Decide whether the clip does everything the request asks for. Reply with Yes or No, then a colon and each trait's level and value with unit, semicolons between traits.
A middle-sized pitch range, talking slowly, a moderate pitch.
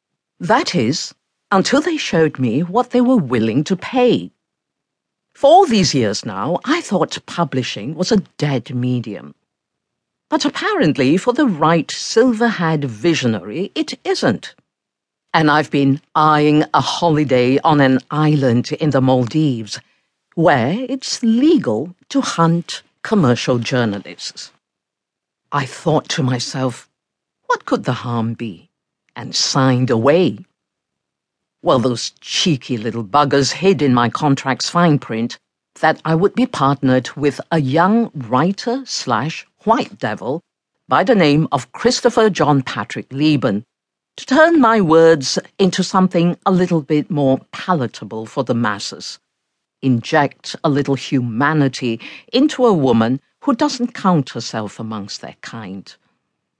No: wide, 7.4 semitones; slow, 130 wpm; medium, 150 Hz